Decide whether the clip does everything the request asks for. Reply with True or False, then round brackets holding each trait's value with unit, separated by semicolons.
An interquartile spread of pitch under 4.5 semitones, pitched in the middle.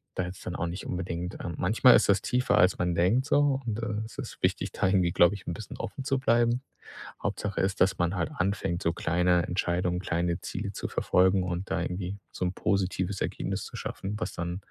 False (2.6 semitones; 95 Hz)